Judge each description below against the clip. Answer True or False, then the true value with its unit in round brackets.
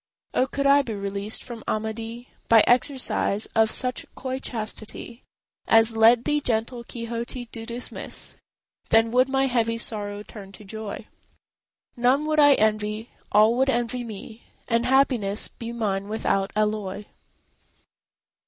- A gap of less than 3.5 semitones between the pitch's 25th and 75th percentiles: True (2.7 semitones)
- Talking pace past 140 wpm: False (135 wpm)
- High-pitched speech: True (230 Hz)